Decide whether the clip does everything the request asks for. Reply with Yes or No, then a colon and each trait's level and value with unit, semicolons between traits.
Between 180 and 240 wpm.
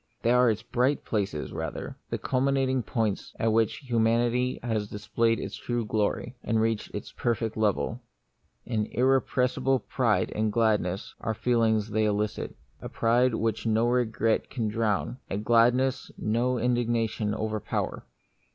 No: average, 150 wpm